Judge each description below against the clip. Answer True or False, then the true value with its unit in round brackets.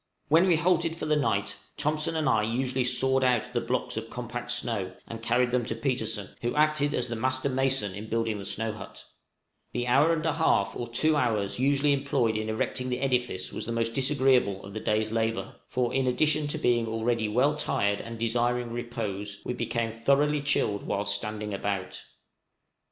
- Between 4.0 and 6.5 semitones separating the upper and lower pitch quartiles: False (3.5 semitones)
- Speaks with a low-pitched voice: True (120 Hz)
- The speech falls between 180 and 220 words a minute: True (190 wpm)